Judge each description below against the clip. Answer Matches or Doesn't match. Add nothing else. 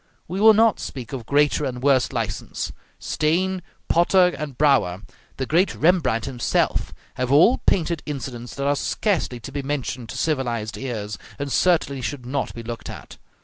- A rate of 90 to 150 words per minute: Doesn't match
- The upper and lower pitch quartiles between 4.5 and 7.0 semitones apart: Matches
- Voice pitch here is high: Doesn't match